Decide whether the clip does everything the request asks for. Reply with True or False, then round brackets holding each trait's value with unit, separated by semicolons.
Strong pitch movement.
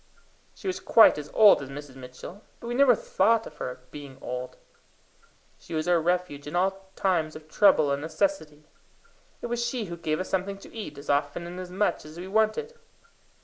True (6.3 semitones)